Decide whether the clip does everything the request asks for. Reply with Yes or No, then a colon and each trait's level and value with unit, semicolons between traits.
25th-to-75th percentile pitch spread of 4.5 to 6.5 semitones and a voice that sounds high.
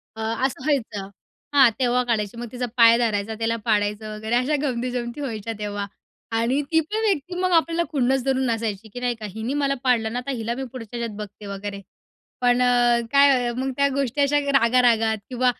No: average, 3.3 semitones; high, 240 Hz